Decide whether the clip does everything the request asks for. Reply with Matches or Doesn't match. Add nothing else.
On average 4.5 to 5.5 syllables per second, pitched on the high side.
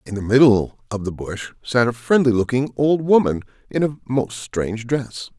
Doesn't match